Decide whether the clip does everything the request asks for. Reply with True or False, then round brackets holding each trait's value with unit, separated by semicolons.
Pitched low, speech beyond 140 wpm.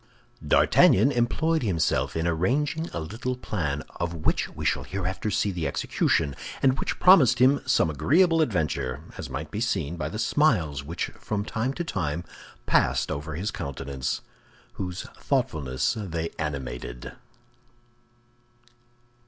False (90 Hz; 135 wpm)